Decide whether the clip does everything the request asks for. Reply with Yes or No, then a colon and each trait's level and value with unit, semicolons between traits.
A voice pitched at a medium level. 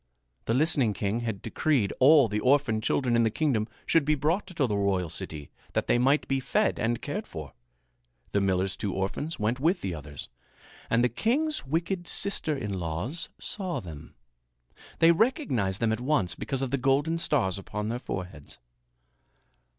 No: low, 120 Hz